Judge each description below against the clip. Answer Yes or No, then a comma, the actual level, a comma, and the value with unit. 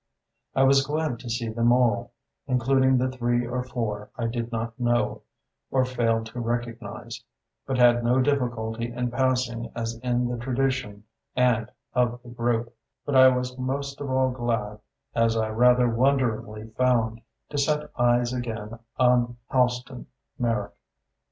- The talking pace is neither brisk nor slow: Yes, average, 150 wpm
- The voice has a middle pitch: No, low, 120 Hz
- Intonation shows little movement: Yes, narrow, 1.7 semitones